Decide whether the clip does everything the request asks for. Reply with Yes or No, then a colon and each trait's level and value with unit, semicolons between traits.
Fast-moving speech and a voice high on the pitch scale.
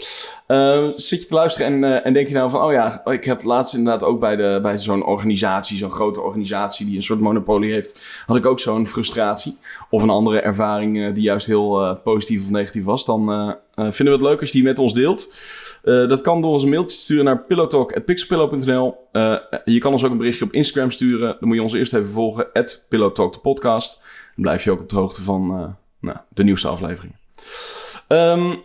No: fast, 230 wpm; low, 120 Hz